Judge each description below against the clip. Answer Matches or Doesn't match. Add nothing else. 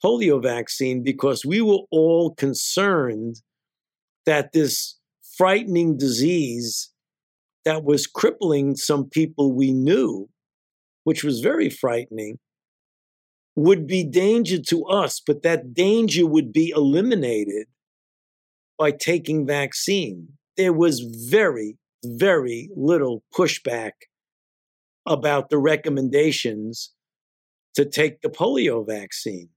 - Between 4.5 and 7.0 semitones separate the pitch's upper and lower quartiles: Matches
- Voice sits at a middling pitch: Matches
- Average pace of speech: Doesn't match